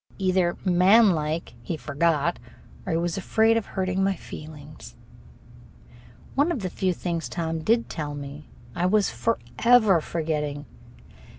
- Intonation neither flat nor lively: Yes, average, 4.2 semitones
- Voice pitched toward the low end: No, medium, 175 Hz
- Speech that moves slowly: Yes, slow, 130 wpm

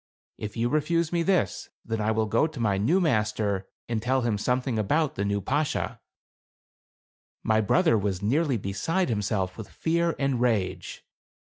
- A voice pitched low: Yes, low, 115 Hz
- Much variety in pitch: Yes, wide, 6.6 semitones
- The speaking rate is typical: Yes, average, 160 wpm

